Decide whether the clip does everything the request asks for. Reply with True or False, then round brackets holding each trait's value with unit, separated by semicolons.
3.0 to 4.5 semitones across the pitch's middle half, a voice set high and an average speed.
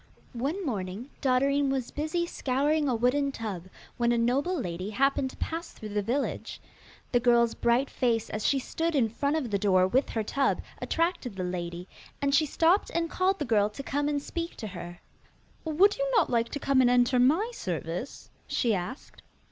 False (5.1 semitones; 255 Hz; 195 wpm)